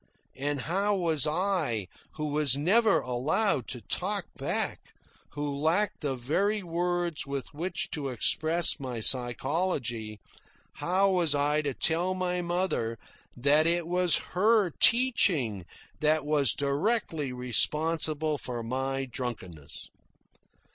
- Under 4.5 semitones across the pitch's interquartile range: No, average, 5.1 semitones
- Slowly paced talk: Yes, slow, 120 wpm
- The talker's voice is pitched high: No, medium, 150 Hz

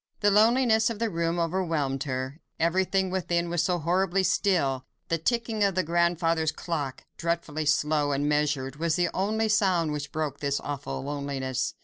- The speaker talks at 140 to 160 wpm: Yes, average, 150 wpm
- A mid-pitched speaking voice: Yes, medium, 165 Hz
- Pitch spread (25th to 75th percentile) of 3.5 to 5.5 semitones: Yes, average, 4.4 semitones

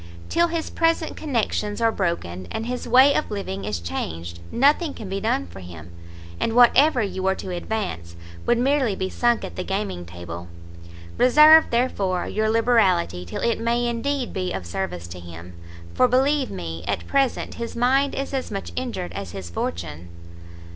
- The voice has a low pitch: No, high, 210 Hz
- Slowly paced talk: No, average, 175 wpm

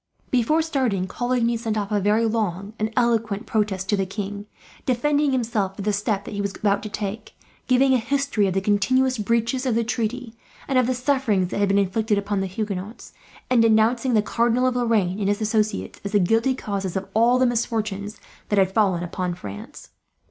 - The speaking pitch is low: No, high, 215 Hz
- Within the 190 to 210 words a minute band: Yes, average, 200 wpm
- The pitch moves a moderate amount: Yes, average, 3.3 semitones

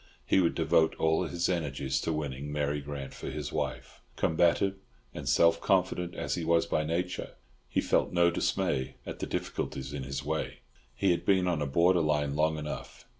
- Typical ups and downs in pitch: Yes, average, 3.1 semitones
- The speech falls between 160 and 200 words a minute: Yes, average, 180 wpm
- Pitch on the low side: Yes, very low, 80 Hz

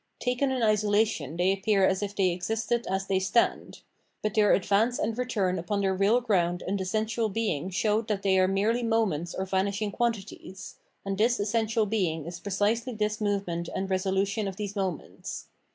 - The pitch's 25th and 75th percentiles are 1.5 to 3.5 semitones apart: Yes, narrow, 2.6 semitones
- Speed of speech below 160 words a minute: No, average, 180 wpm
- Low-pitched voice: No, high, 200 Hz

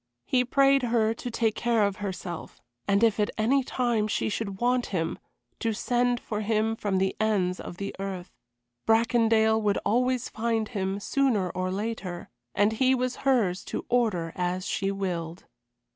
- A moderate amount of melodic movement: Yes, average, 3.7 semitones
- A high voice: Yes, high, 215 Hz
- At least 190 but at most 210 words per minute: No, average, 165 wpm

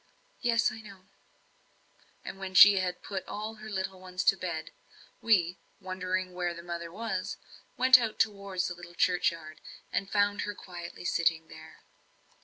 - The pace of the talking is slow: No, average, 155 wpm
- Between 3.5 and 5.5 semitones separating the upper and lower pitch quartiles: No, average, 2.8 semitones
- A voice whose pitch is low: No, medium, 185 Hz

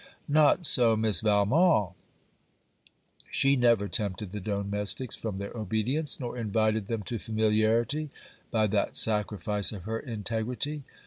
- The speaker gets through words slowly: Yes, slow, 125 wpm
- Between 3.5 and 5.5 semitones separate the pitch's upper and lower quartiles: No, narrow, 2.6 semitones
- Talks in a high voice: No, low, 110 Hz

